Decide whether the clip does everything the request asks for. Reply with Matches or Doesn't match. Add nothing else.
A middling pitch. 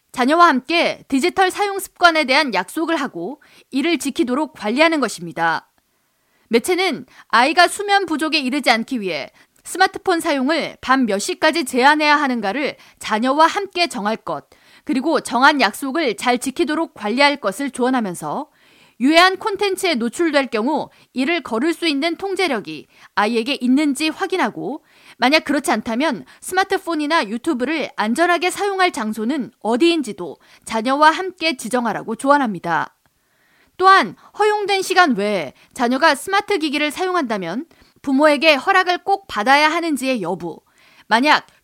Doesn't match